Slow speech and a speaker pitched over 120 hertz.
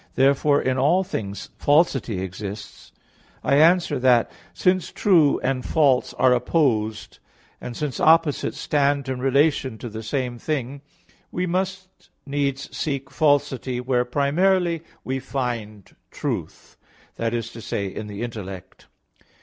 Yes: slow, 130 wpm; low, 135 Hz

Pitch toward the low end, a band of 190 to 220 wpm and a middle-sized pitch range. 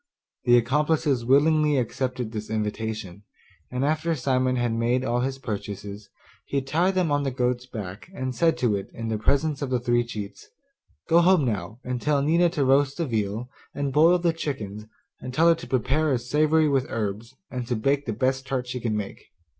Yes: low, 130 Hz; average, 200 wpm; average, 4.4 semitones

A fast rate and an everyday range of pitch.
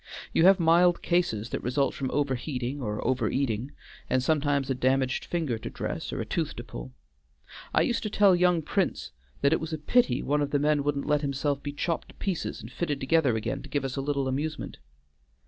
Yes: fast, 215 wpm; average, 3.7 semitones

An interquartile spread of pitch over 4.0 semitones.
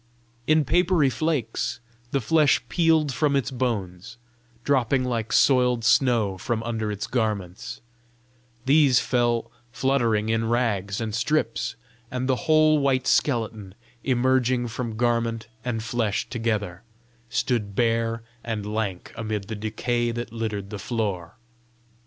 No: average, 3.0 semitones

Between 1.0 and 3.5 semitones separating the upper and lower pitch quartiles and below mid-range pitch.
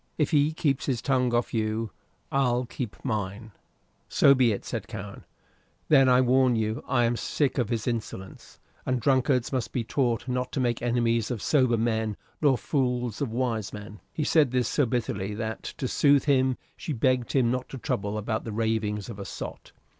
Yes: average, 2.8 semitones; low, 120 Hz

